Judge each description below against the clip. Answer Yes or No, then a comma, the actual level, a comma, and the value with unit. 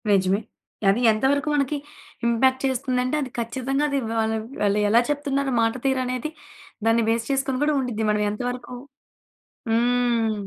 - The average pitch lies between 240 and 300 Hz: Yes, high, 245 Hz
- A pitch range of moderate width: Yes, average, 3.1 semitones